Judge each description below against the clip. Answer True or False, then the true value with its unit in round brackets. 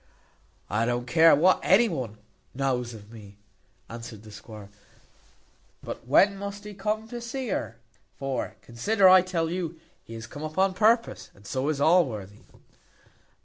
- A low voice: False (145 Hz)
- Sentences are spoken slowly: False (150 wpm)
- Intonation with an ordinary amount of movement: False (8.9 semitones)